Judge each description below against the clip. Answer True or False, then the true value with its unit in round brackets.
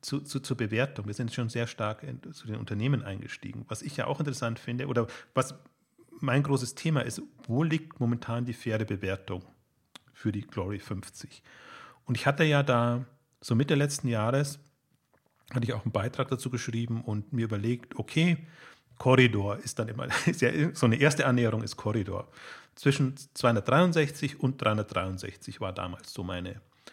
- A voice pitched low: True (125 Hz)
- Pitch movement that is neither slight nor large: True (4.1 semitones)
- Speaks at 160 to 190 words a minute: True (165 wpm)